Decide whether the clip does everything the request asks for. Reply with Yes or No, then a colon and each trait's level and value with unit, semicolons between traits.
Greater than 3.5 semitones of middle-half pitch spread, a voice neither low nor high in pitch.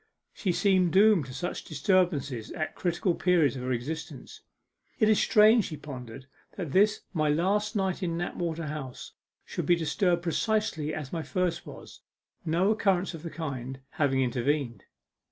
Yes: average, 4.6 semitones; medium, 165 Hz